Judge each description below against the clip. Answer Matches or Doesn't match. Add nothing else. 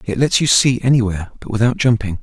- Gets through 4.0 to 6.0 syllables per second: Doesn't match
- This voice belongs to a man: Matches